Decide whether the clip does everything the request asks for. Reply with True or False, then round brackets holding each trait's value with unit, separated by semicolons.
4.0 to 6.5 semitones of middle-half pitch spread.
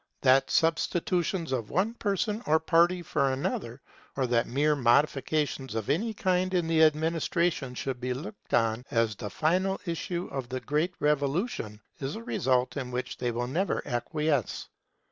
True (5.4 semitones)